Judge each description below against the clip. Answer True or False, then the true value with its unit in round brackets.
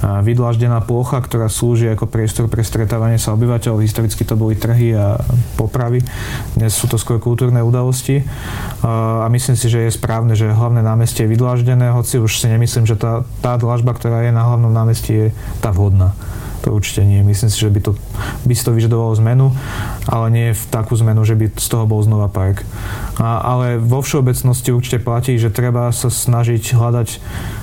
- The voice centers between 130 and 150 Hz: False (115 Hz)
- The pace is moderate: False (185 wpm)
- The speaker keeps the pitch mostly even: True (1.7 semitones)